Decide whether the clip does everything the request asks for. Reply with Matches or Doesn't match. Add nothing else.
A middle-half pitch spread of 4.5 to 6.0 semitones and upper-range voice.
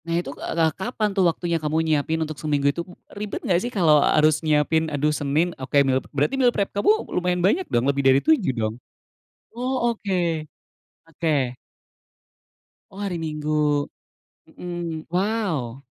Doesn't match